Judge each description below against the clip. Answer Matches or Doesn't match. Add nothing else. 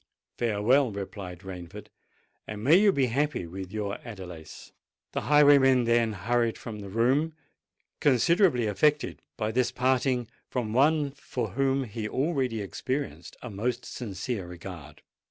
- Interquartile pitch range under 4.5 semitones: Doesn't match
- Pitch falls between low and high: Doesn't match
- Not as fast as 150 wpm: Matches